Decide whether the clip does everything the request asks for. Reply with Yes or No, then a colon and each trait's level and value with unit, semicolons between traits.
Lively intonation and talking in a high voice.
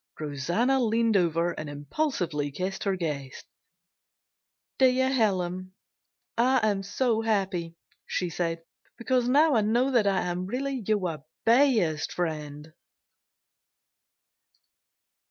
Yes: wide, 6.3 semitones; high, 195 Hz